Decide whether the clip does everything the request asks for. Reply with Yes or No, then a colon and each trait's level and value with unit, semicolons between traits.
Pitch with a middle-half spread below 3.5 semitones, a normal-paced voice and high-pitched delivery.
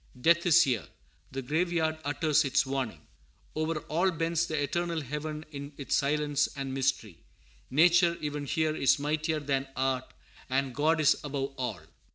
No: average, 2.8 semitones; average, 155 wpm; medium, 150 Hz